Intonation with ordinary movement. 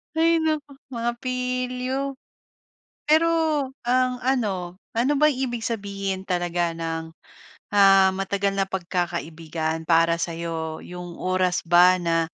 No: wide, 6.7 semitones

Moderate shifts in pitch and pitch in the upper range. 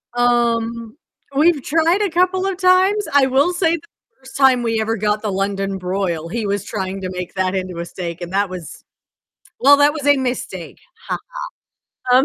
No: wide, 7.1 semitones; high, 235 Hz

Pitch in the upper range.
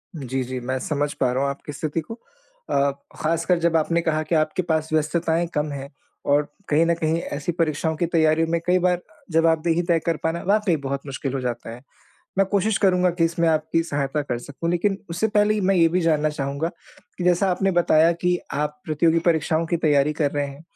No: medium, 160 Hz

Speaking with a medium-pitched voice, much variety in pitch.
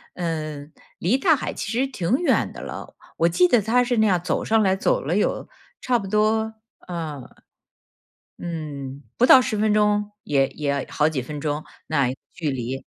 Yes: medium, 180 Hz; wide, 6.9 semitones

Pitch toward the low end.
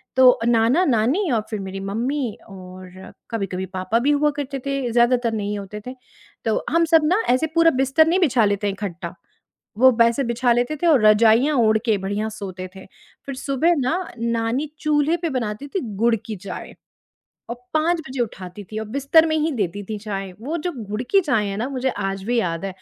No: high, 235 Hz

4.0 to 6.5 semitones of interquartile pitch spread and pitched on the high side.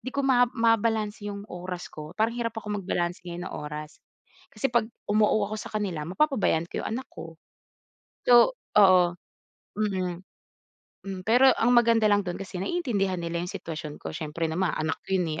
Yes: average, 4.6 semitones; high, 195 Hz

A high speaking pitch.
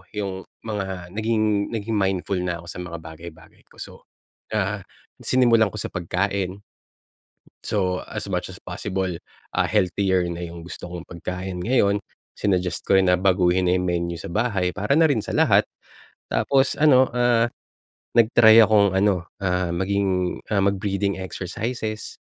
No: very low, 95 Hz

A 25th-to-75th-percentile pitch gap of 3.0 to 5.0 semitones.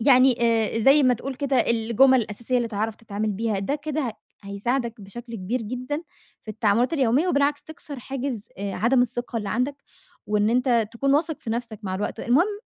Yes: average, 3.7 semitones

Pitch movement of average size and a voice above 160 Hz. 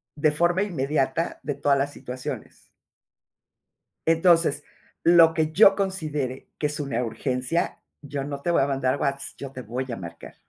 No: average, 3.7 semitones; medium, 145 Hz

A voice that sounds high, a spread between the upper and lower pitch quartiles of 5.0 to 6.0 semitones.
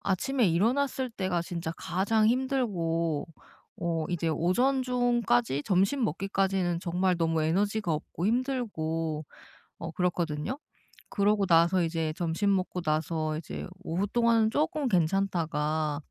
No: medium, 180 Hz; wide, 5.4 semitones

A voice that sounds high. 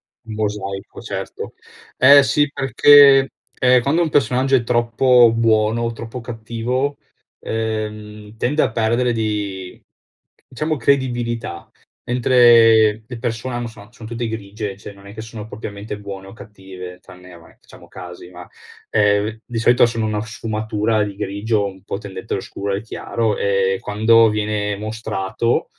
No: low, 110 Hz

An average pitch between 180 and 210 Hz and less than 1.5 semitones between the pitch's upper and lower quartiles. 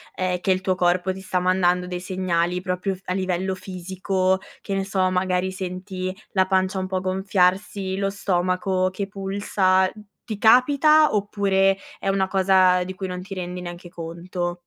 Yes: medium, 185 Hz; narrow, 1.1 semitones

